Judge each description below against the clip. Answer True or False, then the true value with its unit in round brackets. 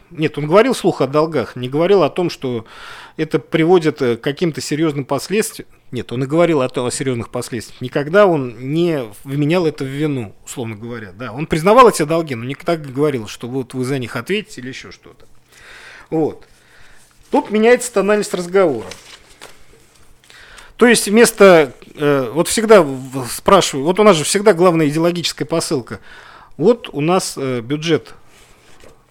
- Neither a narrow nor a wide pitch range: False (6.0 semitones)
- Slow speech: False (160 wpm)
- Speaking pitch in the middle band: True (155 Hz)